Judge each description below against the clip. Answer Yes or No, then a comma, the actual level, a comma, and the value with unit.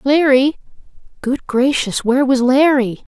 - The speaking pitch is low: No, very high, 265 Hz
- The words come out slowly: Yes, slow, 115 wpm